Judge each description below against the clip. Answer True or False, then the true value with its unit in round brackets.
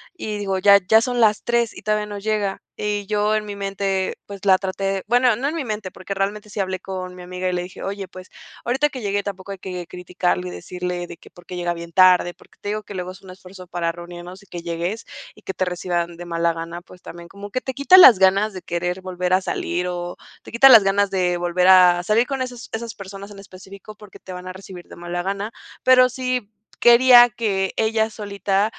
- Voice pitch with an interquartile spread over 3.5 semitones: False (2.9 semitones)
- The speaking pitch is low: False (195 Hz)